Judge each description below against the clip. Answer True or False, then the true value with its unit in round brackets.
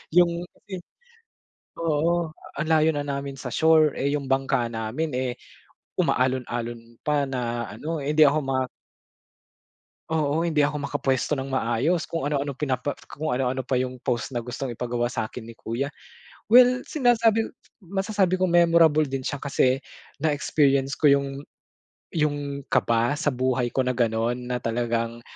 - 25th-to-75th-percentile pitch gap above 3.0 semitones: True (3.9 semitones)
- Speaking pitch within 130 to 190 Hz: True (140 Hz)